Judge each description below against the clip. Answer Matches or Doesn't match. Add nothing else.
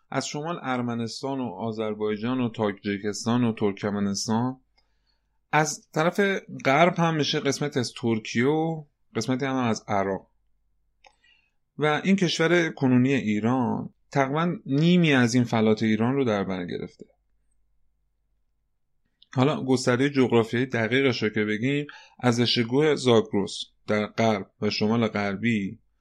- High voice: Doesn't match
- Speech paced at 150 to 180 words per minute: Doesn't match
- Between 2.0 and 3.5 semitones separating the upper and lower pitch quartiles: Doesn't match